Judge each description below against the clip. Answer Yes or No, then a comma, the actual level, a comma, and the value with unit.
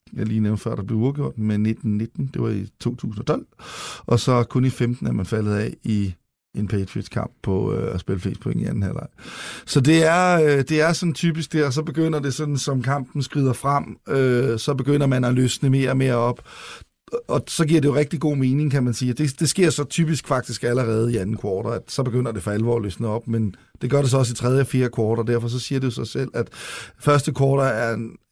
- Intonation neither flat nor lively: Yes, average, 3.9 semitones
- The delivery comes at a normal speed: No, fast, 245 wpm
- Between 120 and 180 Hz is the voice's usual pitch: Yes, low, 130 Hz